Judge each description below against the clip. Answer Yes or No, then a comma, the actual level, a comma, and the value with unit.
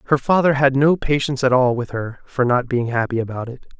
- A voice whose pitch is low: Yes, low, 130 Hz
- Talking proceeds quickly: Yes, fast, 235 wpm